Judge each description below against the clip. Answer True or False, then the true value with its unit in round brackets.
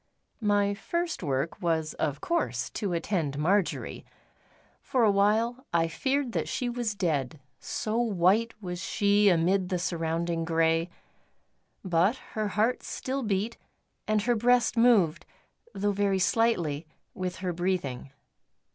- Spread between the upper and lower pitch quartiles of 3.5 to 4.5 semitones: False (5.1 semitones)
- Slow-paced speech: True (130 wpm)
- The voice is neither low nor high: False (195 Hz)